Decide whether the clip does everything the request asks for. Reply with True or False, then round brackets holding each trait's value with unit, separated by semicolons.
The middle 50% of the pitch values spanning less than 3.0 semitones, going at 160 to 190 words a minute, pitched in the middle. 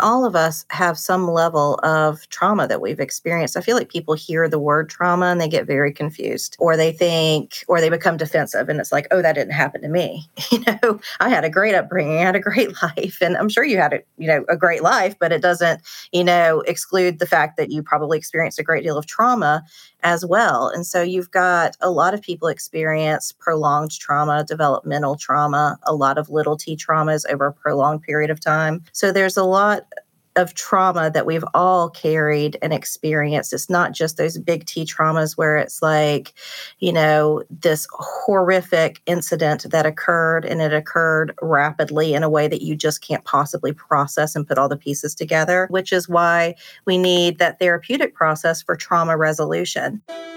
False (2.6 semitones; 200 wpm; 165 Hz)